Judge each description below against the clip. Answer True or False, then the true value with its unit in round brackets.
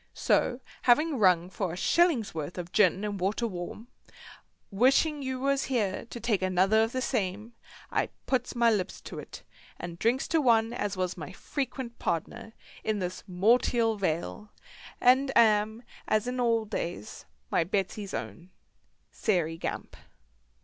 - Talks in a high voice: True (215 Hz)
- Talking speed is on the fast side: False (155 wpm)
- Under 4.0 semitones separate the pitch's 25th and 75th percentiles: False (4.8 semitones)